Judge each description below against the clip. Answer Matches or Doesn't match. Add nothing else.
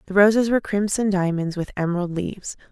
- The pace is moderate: Matches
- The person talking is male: Doesn't match